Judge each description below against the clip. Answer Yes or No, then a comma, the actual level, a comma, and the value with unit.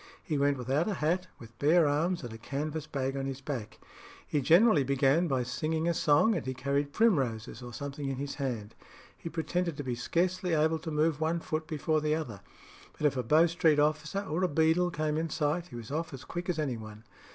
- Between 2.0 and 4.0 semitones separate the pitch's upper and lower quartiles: Yes, average, 3.3 semitones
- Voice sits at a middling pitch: Yes, medium, 150 Hz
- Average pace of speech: No, fast, 220 wpm